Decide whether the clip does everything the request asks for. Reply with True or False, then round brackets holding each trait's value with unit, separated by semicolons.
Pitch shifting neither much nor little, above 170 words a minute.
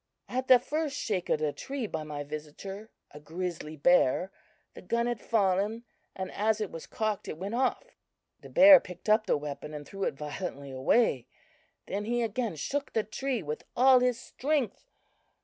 False (7.8 semitones; 180 wpm)